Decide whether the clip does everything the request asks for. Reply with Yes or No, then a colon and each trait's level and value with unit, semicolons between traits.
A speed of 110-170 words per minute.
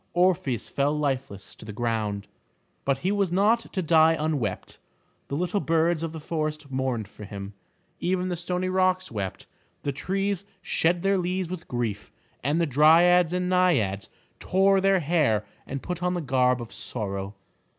Yes: average, 165 wpm